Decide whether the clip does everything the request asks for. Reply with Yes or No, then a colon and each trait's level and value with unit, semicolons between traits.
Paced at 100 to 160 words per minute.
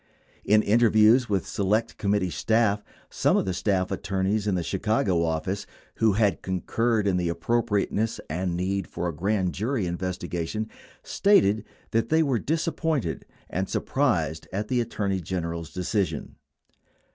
Yes: average, 140 wpm